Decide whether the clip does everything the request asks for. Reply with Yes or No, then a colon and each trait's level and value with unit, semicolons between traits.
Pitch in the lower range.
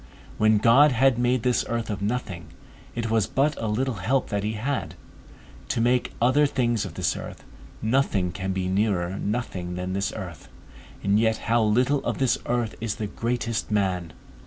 Yes: low, 110 Hz